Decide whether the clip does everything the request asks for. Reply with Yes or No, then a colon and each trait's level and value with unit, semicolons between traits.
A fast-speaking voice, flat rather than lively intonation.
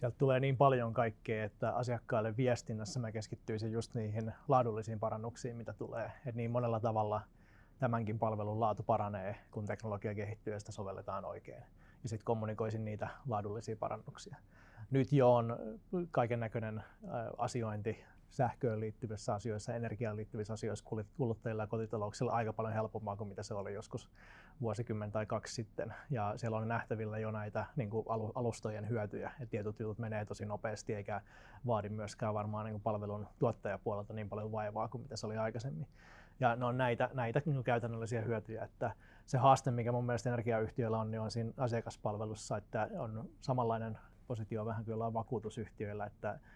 Yes: fast, 160 wpm; narrow, 1.8 semitones